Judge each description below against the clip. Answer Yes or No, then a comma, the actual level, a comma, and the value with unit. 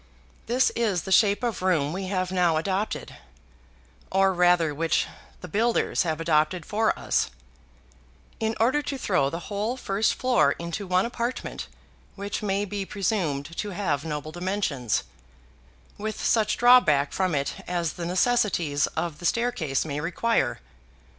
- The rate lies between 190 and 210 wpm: No, average, 145 wpm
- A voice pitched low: No, medium, 185 Hz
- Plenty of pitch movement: No, average, 4.6 semitones